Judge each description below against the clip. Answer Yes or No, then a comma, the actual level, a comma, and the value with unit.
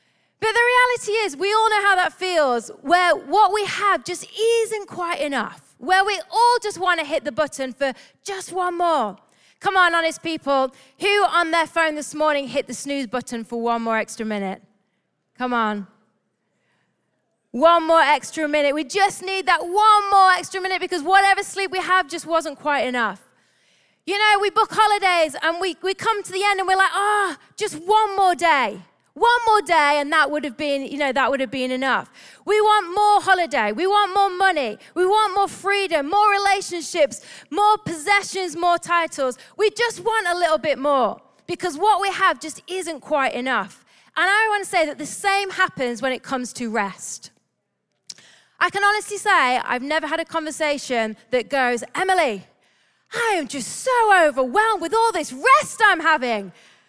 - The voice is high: Yes, very high, 345 Hz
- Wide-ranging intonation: Yes, wide, 6.1 semitones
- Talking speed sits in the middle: Yes, average, 190 wpm